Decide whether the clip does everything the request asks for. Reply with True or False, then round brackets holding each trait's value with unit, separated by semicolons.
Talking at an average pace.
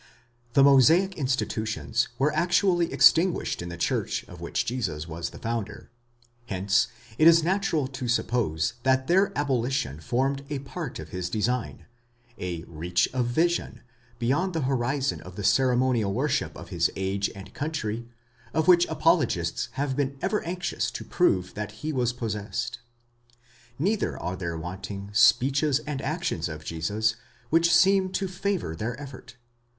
True (150 wpm)